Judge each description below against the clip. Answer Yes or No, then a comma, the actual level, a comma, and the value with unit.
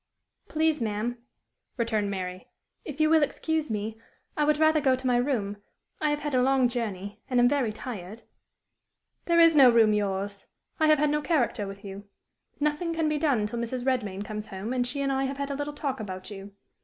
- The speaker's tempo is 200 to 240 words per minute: Yes, fast, 205 wpm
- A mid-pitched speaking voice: No, very high, 250 Hz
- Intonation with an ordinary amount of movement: No, wide, 6.0 semitones